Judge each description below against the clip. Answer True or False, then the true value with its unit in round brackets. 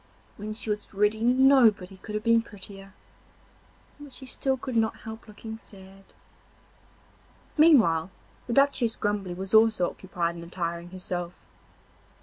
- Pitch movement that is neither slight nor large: True (3.6 semitones)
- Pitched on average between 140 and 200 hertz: False (210 Hz)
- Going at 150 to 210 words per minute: False (135 wpm)